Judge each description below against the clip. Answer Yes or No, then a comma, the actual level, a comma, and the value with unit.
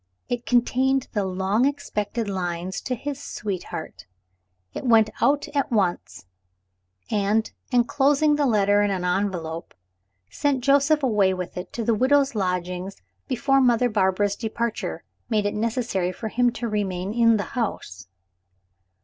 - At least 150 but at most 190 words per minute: No, average, 140 wpm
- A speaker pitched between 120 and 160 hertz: No, high, 215 Hz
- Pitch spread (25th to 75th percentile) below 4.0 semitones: No, average, 4.8 semitones